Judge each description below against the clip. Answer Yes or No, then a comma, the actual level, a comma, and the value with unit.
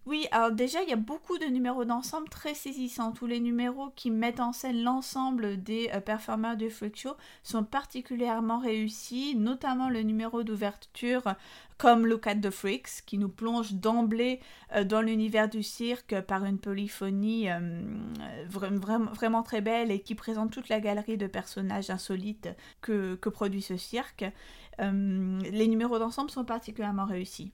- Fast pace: No, average, 170 wpm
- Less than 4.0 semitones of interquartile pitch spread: Yes, average, 2.9 semitones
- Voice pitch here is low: No, high, 225 Hz